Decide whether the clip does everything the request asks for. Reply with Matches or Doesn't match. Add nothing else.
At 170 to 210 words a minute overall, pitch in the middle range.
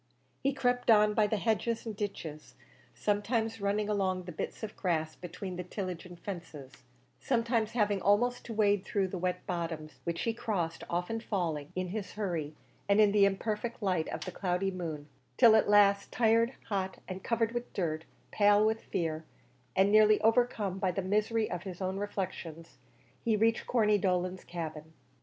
Doesn't match